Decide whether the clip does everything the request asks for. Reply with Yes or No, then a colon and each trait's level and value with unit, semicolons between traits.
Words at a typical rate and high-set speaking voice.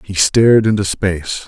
No: average, 165 wpm; low, 100 Hz